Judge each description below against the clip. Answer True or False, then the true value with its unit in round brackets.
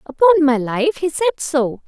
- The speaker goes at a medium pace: True (190 wpm)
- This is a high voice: True (300 Hz)